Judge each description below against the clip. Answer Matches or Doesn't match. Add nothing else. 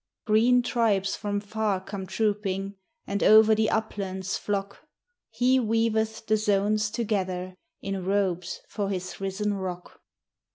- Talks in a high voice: Matches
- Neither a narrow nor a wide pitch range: Doesn't match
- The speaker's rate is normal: Doesn't match